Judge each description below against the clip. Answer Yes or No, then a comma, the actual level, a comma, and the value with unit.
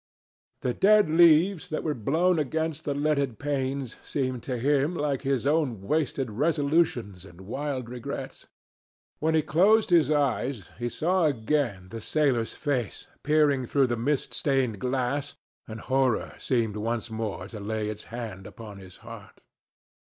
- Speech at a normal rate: Yes, average, 150 wpm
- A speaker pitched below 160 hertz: Yes, low, 135 Hz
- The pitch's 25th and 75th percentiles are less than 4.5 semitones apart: No, average, 4.9 semitones